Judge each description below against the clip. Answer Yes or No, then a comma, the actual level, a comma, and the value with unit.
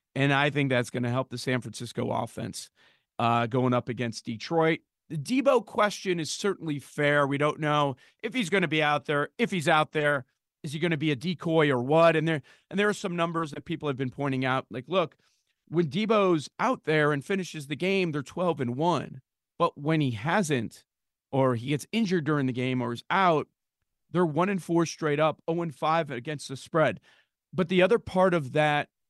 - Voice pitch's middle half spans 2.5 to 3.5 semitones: No, average, 4.7 semitones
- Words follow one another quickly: Yes, fast, 215 wpm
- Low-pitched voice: No, medium, 150 Hz